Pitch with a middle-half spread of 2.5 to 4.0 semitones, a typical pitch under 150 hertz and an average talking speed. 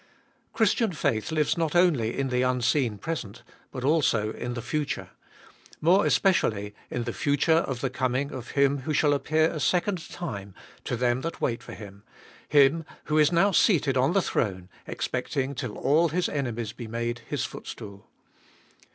No: average, 5.1 semitones; low, 135 Hz; average, 170 wpm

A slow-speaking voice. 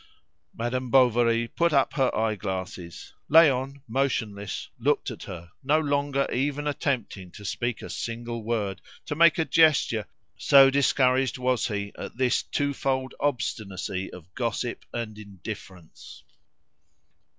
Yes: slow, 130 wpm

